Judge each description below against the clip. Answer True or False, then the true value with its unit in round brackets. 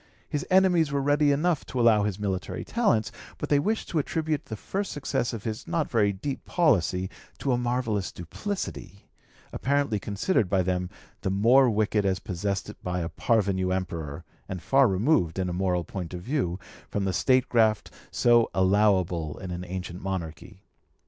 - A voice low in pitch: True (105 Hz)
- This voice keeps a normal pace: True (170 wpm)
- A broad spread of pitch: True (6.7 semitones)